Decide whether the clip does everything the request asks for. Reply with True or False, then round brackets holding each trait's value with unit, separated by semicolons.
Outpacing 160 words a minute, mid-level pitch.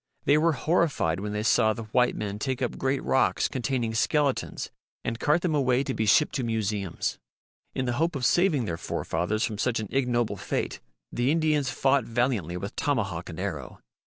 False (190 wpm; 120 Hz)